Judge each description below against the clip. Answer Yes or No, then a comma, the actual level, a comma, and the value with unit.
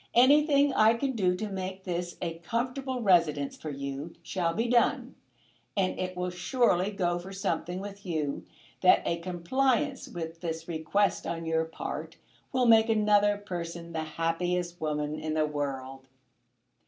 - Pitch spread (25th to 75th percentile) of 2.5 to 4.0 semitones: No, average, 4.5 semitones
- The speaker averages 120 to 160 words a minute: Yes, average, 155 wpm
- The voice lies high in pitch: No, medium, 180 Hz